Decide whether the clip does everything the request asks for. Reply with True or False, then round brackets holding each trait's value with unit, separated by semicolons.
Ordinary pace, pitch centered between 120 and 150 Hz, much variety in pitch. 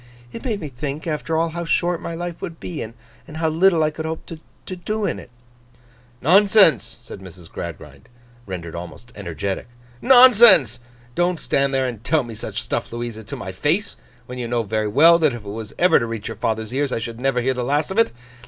False (210 wpm; 140 Hz; 7.0 semitones)